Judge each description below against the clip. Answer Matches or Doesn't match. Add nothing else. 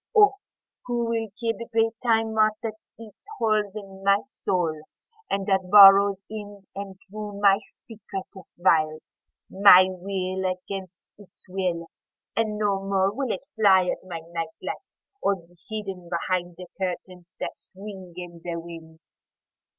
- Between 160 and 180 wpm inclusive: Doesn't match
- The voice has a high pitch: Matches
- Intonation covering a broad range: Doesn't match